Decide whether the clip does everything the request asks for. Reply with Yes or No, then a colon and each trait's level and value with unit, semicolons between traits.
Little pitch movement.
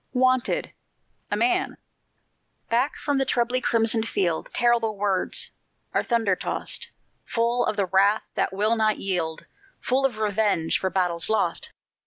No: average, 3.8 semitones